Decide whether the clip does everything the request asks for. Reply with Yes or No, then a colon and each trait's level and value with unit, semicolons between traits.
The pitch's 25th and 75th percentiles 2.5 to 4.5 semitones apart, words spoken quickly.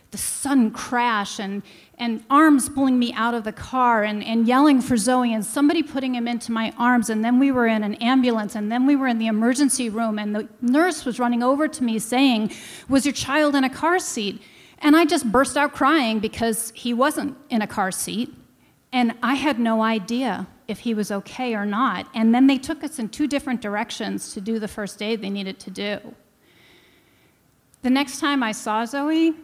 Yes: average, 3.7 semitones; fast, 210 wpm